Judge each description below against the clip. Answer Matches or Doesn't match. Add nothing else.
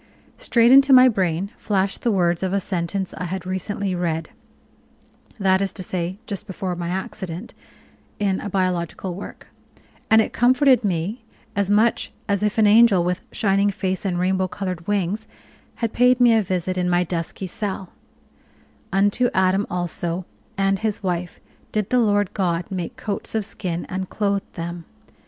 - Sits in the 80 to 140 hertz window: Doesn't match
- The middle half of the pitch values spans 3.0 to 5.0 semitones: Doesn't match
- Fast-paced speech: Doesn't match